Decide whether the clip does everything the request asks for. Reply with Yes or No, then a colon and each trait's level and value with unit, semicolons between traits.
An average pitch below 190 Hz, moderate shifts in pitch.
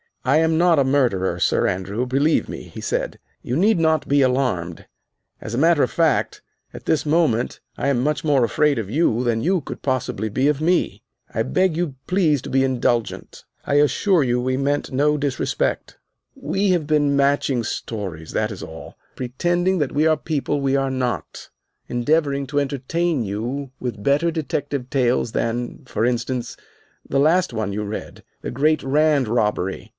Yes: medium, 140 Hz; average, 4.2 semitones